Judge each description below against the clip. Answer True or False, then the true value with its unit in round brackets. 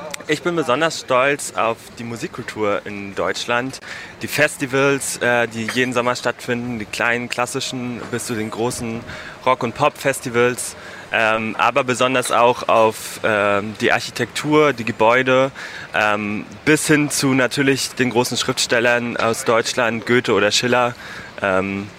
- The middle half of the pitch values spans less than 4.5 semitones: True (2.8 semitones)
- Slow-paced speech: True (125 wpm)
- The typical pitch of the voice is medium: False (120 Hz)